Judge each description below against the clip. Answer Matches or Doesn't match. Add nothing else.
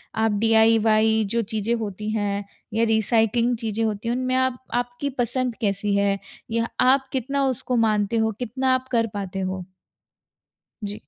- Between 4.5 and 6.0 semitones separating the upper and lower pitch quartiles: Doesn't match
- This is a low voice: Doesn't match